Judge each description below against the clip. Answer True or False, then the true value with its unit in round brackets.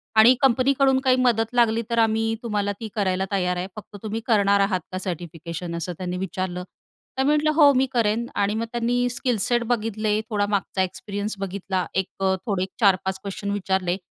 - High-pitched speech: True (205 Hz)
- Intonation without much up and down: False (3.7 semitones)